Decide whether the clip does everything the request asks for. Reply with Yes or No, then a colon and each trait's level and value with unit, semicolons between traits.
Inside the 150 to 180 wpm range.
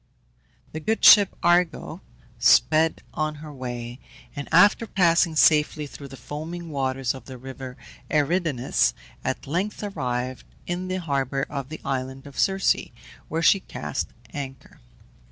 No: slow, 135 wpm